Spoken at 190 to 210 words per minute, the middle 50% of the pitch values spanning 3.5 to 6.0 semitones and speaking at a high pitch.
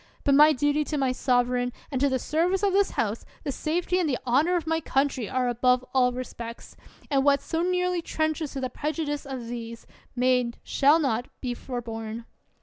Yes: average, 195 wpm; average, 4.1 semitones; very high, 270 Hz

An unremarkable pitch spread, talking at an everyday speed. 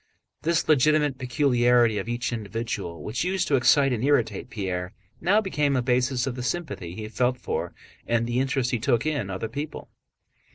Yes: average, 3.9 semitones; average, 175 wpm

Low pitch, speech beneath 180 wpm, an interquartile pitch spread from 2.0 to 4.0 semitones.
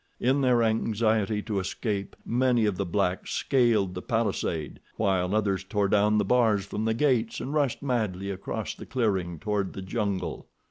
Yes: low, 105 Hz; average, 170 wpm; average, 3.2 semitones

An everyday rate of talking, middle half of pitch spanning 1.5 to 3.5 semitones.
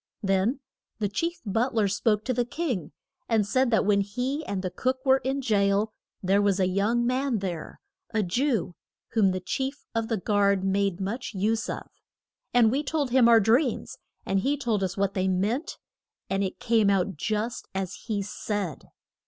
No: average, 185 wpm; average, 4.1 semitones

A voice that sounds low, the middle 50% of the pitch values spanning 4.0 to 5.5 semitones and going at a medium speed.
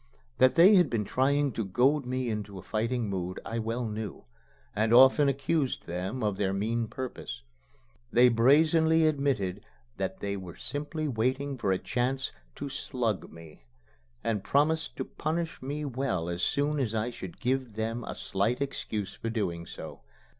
Yes: low, 120 Hz; average, 5.1 semitones; average, 165 wpm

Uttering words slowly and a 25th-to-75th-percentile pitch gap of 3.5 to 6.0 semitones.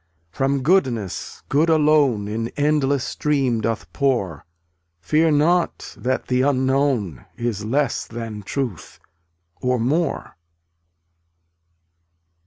Yes: slow, 95 wpm; average, 4.4 semitones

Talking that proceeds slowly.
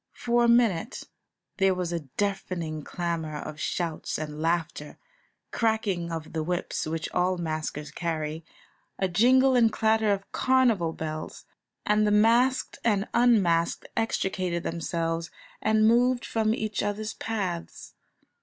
Yes: slow, 130 wpm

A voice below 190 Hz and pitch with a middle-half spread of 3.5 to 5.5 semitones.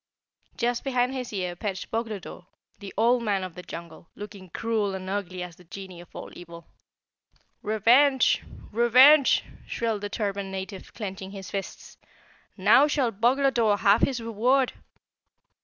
No: high, 210 Hz; average, 3.9 semitones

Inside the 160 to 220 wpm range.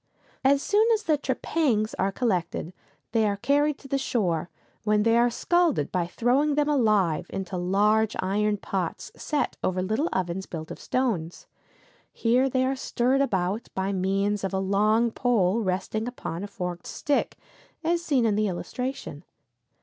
Yes: average, 165 wpm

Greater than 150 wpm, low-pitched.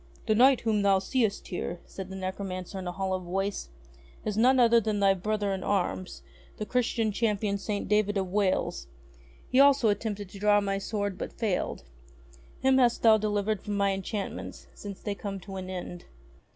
No: average, 185 wpm; high, 205 Hz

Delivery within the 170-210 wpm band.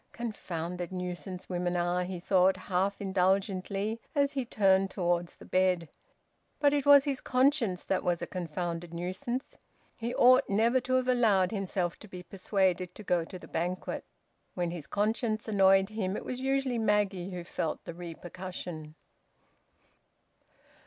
No: average, 150 wpm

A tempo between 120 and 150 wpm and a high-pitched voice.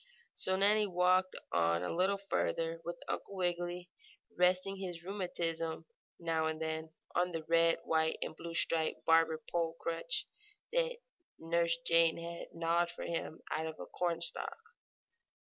No: average, 145 wpm; medium, 170 Hz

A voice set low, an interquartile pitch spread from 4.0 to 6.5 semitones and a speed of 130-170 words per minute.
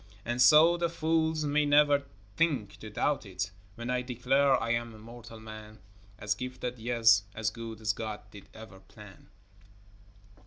Yes: low, 120 Hz; average, 4.6 semitones; average, 160 wpm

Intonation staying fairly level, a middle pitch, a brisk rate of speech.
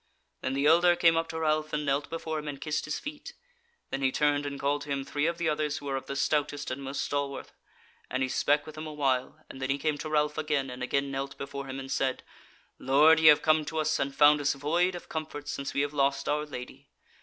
Yes: narrow, 2.0 semitones; medium, 145 Hz; fast, 250 wpm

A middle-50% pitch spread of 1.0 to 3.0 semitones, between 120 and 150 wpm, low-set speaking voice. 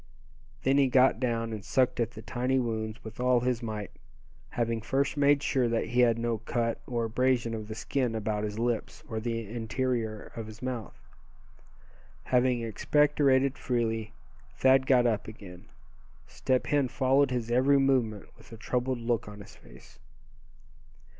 No: narrow, 2.6 semitones; average, 160 wpm; low, 120 Hz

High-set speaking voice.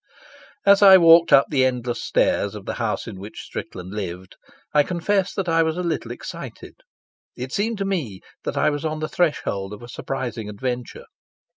No: medium, 140 Hz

